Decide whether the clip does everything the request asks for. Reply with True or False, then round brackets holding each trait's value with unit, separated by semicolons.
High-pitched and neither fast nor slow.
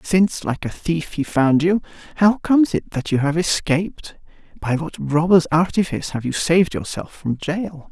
False (165 Hz; 175 wpm)